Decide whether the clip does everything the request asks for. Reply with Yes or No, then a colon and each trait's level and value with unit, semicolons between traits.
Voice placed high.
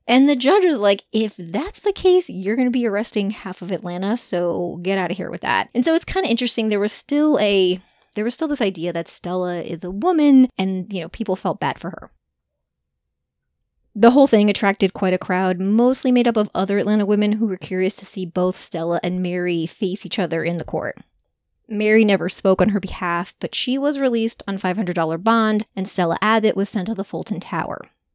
Yes: high, 195 Hz